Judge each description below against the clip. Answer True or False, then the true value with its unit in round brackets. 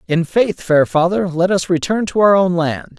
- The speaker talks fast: True (220 wpm)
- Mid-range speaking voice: True (180 Hz)